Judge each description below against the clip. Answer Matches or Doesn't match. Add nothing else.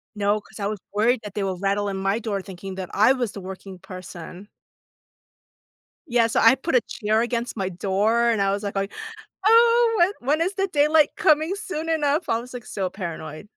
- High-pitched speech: Matches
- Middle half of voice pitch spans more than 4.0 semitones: Matches